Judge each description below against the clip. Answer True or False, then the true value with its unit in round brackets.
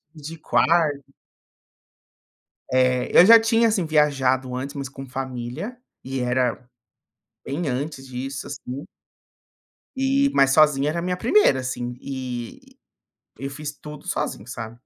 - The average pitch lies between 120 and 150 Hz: True (135 Hz)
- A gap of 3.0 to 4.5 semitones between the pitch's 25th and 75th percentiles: True (4.2 semitones)